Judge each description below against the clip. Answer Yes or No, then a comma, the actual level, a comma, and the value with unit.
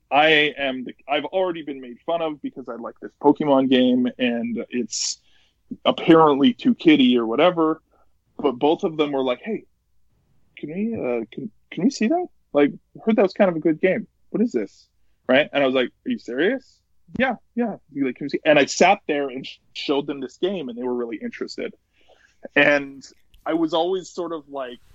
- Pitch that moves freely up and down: Yes, wide, 6.8 semitones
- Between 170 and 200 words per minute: Yes, average, 190 wpm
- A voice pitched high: No, medium, 145 Hz